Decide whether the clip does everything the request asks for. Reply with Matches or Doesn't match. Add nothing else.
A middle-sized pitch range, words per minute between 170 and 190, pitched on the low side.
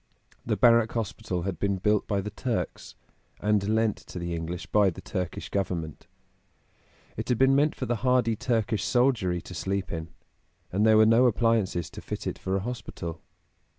Matches